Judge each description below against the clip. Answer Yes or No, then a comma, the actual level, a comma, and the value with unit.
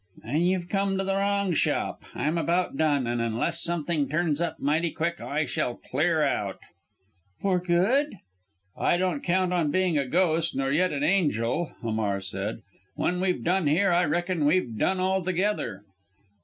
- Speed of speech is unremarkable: Yes, average, 165 wpm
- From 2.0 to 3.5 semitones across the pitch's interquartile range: No, average, 4.4 semitones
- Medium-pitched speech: Yes, medium, 170 Hz